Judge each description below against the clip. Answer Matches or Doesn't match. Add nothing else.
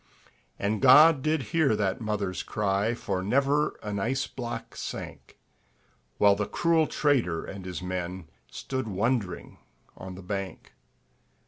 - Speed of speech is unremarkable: Doesn't match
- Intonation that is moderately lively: Doesn't match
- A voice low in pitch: Matches